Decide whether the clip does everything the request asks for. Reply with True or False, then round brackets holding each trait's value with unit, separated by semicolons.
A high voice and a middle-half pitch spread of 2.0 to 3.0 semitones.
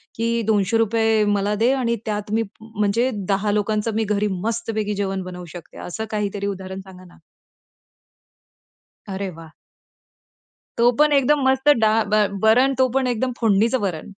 True (215 Hz; 2.5 semitones)